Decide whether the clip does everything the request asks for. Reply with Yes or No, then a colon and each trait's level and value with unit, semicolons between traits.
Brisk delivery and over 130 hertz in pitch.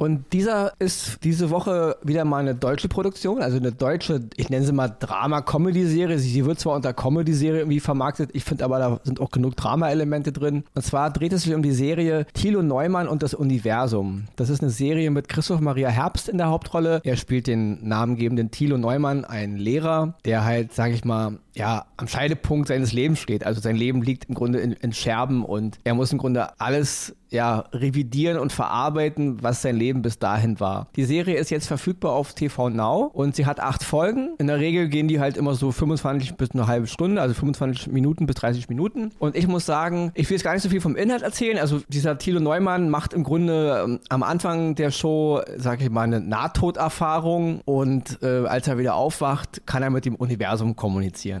Yes: fast, 205 wpm; medium, 140 Hz